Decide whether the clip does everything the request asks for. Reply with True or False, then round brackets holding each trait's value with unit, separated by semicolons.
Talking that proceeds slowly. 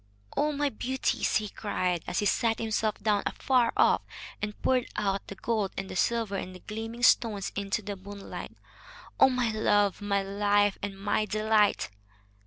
False (170 wpm)